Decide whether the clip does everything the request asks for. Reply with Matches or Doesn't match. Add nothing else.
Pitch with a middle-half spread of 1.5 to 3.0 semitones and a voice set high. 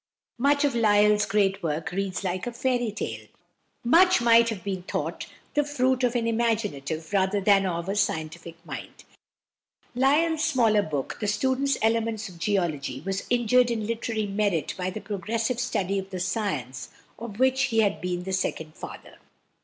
Doesn't match